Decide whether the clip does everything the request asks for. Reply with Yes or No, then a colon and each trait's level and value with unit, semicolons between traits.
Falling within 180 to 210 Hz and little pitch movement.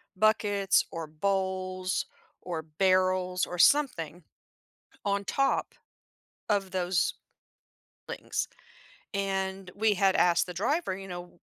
Yes: high, 190 Hz; narrow, 1.7 semitones